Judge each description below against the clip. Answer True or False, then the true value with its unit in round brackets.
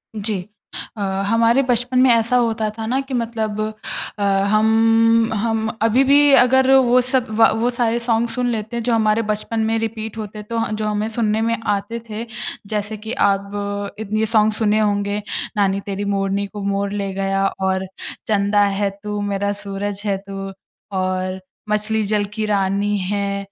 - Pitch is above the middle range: True (215 Hz)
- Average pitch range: False (2.1 semitones)